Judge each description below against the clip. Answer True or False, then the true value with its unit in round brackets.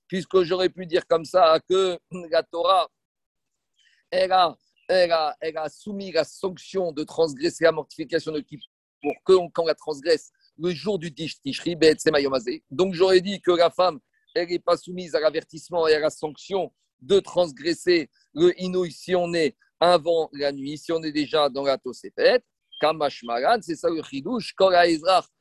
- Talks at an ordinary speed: True (170 wpm)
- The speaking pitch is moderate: True (170 Hz)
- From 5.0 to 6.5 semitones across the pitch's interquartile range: False (3.2 semitones)